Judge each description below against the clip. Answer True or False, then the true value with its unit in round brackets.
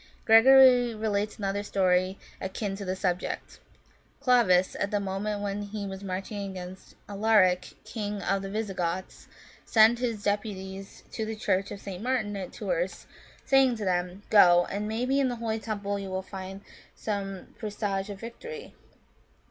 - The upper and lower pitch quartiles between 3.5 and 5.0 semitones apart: False (2.5 semitones)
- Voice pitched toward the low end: False (205 Hz)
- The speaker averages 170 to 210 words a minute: False (160 wpm)